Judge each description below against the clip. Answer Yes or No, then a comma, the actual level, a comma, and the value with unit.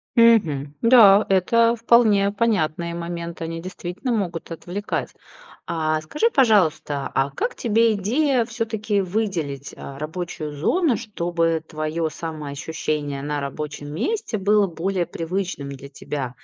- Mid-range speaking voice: Yes, medium, 175 Hz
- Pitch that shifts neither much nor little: No, wide, 5.9 semitones